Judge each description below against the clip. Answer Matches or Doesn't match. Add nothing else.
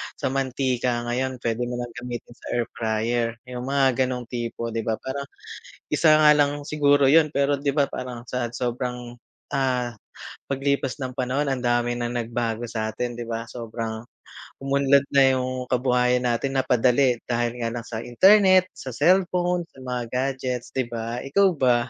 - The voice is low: Matches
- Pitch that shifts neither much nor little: Doesn't match